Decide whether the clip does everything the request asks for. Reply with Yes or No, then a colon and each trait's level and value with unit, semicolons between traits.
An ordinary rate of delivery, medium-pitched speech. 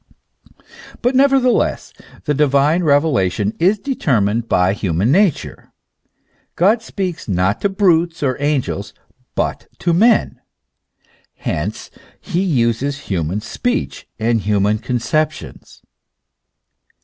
No: slow, 105 wpm; medium, 145 Hz